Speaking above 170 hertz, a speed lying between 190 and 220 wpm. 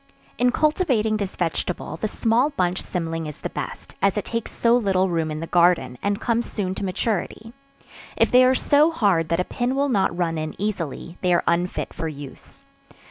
Yes: high, 190 Hz; average, 195 wpm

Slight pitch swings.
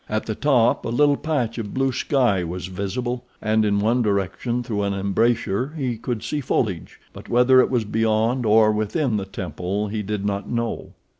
No: average, 3.4 semitones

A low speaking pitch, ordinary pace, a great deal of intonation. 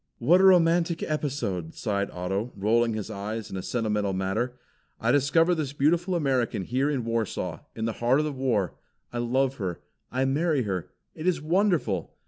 Yes: low, 125 Hz; average, 175 wpm; wide, 6.5 semitones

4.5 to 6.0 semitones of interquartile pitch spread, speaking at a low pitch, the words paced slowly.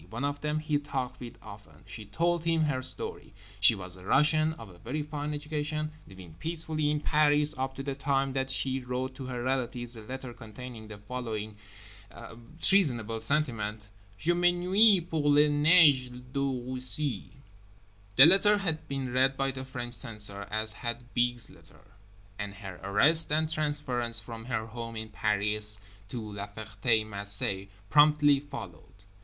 No: average, 5.3 semitones; low, 130 Hz; average, 160 wpm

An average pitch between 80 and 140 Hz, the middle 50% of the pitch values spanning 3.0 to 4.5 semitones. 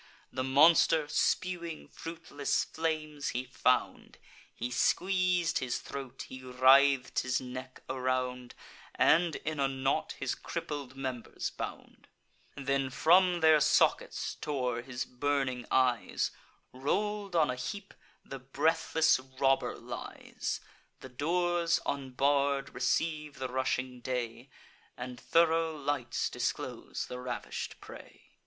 Yes: low, 135 Hz; average, 3.8 semitones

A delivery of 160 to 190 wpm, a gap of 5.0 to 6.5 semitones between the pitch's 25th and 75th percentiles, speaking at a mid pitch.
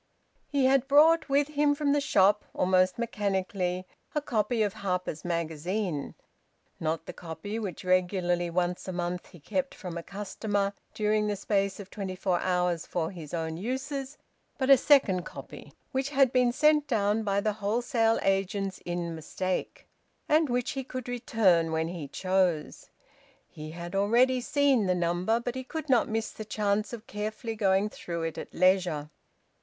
No: average, 165 wpm; wide, 5.4 semitones; high, 200 Hz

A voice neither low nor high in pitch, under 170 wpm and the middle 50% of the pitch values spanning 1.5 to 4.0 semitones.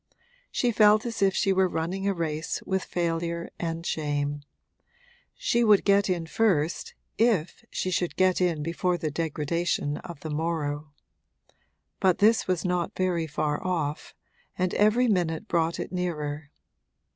Yes: medium, 175 Hz; average, 145 wpm; average, 3.1 semitones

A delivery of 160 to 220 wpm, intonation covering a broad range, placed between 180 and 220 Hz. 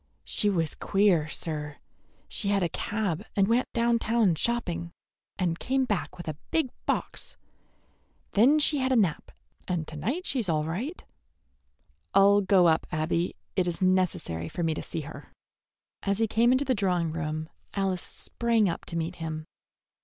Yes: average, 170 wpm; wide, 5.7 semitones; medium, 185 Hz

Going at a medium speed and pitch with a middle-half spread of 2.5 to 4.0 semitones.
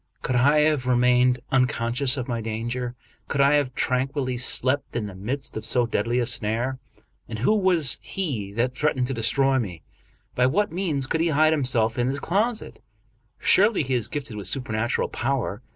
Yes: average, 185 wpm; average, 3.3 semitones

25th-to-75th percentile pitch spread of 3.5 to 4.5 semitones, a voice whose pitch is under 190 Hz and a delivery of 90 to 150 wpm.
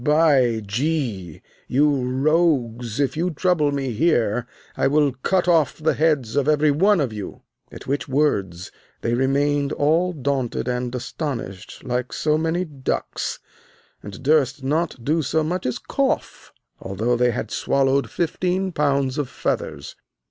Yes: average, 4.1 semitones; medium, 140 Hz; average, 140 wpm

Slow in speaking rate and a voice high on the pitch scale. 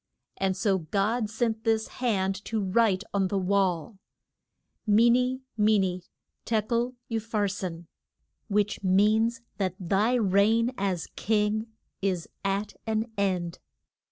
Yes: slow, 130 wpm; high, 205 Hz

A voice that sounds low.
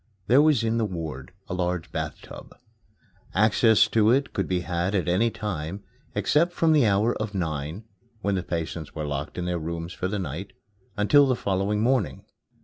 Yes: very low, 95 Hz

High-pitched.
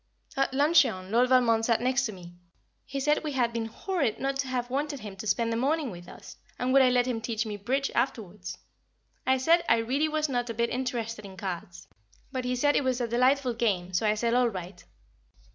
Yes: high, 245 Hz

